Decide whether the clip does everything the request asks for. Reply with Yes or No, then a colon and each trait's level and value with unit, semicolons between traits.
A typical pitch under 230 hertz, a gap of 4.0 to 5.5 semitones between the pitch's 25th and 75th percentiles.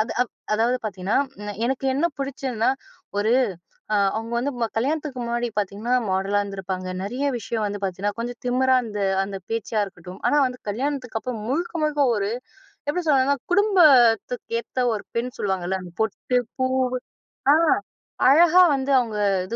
No: high, 240 Hz; average, 4.7 semitones